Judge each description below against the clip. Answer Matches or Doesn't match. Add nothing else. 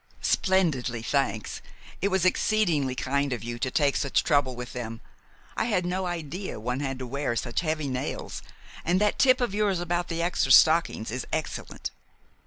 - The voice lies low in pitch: Doesn't match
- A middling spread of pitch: Doesn't match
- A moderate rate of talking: Matches